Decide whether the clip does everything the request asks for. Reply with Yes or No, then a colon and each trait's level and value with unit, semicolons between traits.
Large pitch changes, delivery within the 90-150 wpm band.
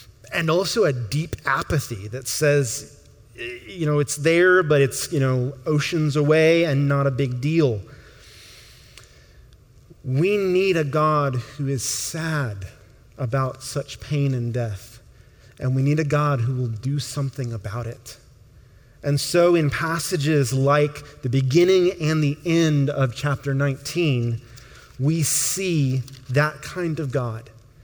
No: average, 3.6 semitones; average, 140 wpm